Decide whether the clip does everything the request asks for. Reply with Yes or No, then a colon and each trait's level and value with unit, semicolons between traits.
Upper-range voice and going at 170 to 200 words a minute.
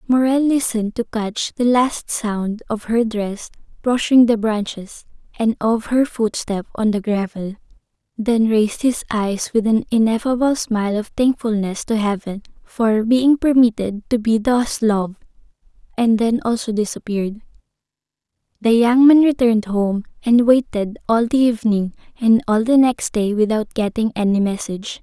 No: high, 225 Hz; average, 150 wpm